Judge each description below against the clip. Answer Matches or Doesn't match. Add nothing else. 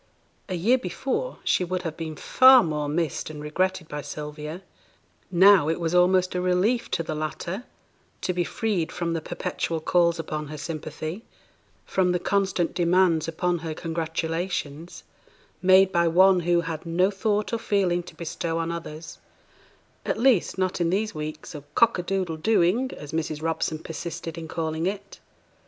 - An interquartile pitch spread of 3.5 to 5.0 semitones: Doesn't match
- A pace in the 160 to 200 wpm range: Matches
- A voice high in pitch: Doesn't match